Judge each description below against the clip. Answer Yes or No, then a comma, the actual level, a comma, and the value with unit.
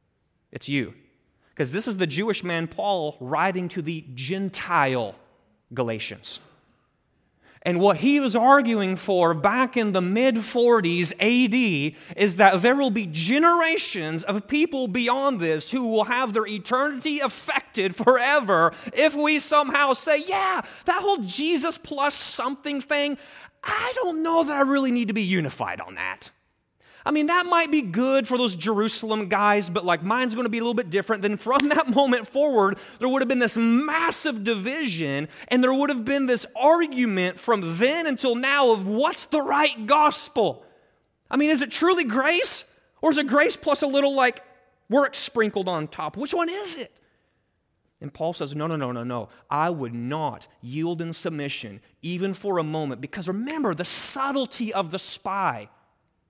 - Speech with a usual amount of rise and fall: No, wide, 7.5 semitones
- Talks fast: No, average, 170 wpm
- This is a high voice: Yes, high, 235 Hz